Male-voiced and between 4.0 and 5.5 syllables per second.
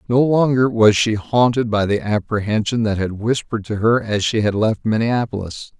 Yes: male; 5.0 syllables/s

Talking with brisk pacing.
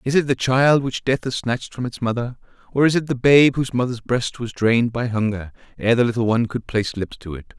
Yes: fast, 255 wpm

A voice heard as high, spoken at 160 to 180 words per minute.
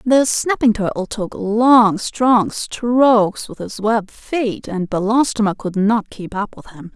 Yes: high, 220 Hz; average, 165 wpm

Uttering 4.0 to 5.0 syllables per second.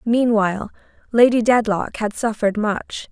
Yes: 4.6 syllables/s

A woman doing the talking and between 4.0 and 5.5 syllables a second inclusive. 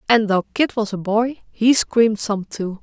Yes: female; 4.4 syllables/s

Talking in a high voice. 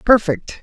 Yes: high, 195 Hz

